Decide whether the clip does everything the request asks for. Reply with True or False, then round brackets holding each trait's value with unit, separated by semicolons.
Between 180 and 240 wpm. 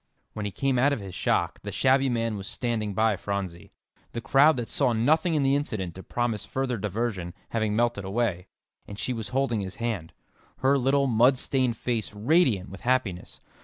True (190 wpm)